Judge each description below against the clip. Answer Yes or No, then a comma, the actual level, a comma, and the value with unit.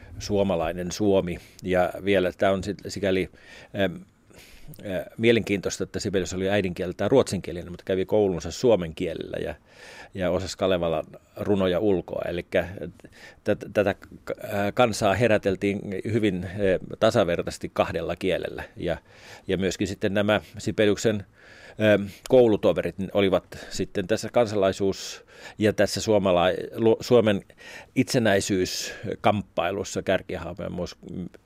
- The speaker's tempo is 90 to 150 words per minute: Yes, average, 100 wpm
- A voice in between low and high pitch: No, low, 100 Hz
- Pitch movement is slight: Yes, narrow, 2.0 semitones